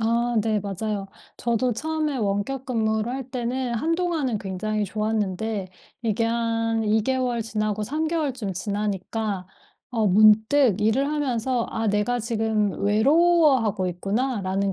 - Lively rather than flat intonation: No, average, 3.5 semitones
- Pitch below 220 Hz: No, high, 225 Hz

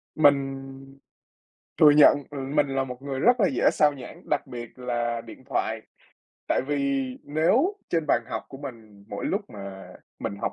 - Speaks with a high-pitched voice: No, low, 135 Hz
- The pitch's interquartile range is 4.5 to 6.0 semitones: No, average, 3.5 semitones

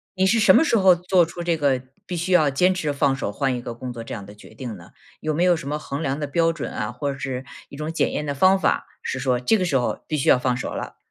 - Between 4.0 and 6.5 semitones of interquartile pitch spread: Yes, average, 5.2 semitones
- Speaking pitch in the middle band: Yes, medium, 145 Hz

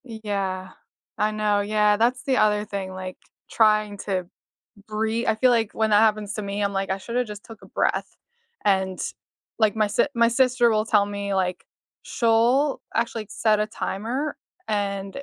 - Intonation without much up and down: Yes, narrow, 2.2 semitones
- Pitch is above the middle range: Yes, high, 215 Hz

